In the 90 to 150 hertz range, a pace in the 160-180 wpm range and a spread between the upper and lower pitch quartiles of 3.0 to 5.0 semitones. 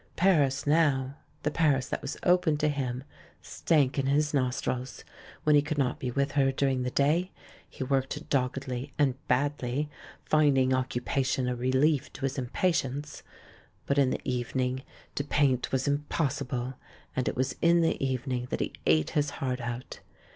No: low, 135 Hz; average, 175 wpm; narrow, 2.4 semitones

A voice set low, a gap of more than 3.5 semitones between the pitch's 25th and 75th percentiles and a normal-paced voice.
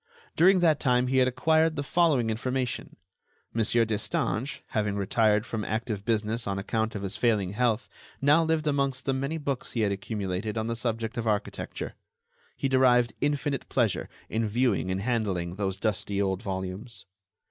Yes: low, 115 Hz; average, 4.2 semitones; average, 165 wpm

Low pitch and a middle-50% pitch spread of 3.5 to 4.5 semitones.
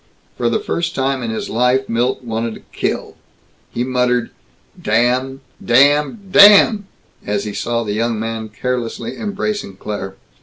Yes: low, 125 Hz; average, 4.1 semitones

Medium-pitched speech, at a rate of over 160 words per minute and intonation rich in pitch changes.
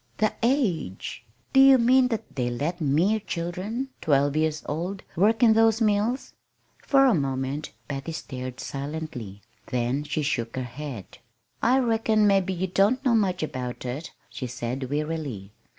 No: medium, 160 Hz; average, 150 wpm; wide, 8.4 semitones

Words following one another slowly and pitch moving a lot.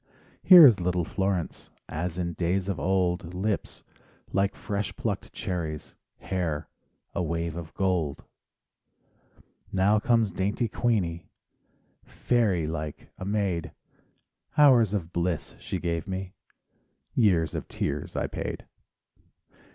No: slow, 115 wpm; average, 3.3 semitones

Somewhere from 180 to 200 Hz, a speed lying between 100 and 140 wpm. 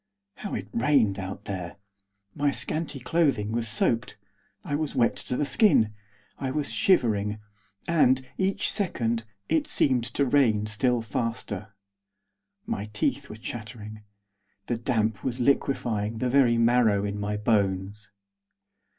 No: low, 115 Hz; slow, 135 wpm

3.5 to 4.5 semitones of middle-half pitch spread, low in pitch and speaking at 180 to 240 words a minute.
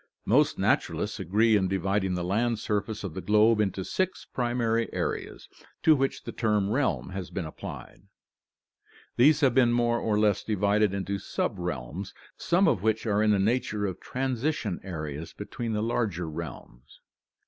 No: average, 3.8 semitones; low, 105 Hz; average, 160 wpm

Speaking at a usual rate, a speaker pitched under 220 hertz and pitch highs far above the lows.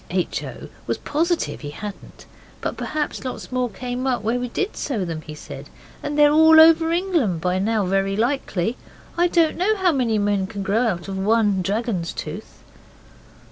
No: average, 180 wpm; high, 230 Hz; wide, 7.5 semitones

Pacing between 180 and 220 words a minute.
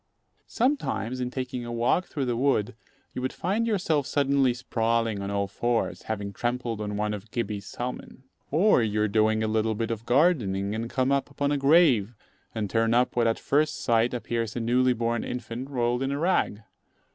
Yes: average, 190 wpm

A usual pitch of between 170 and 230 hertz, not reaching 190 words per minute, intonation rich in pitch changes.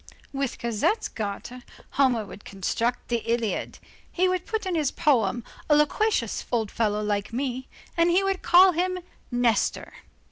No: very high, 250 Hz; average, 150 wpm; wide, 7.5 semitones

